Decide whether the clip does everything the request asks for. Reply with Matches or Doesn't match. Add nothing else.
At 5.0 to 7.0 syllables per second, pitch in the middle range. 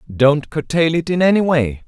Doesn't match